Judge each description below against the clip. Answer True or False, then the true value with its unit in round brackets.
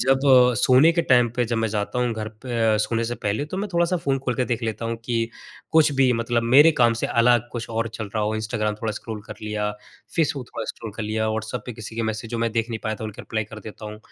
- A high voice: False (115 Hz)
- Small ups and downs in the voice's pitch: True (2.3 semitones)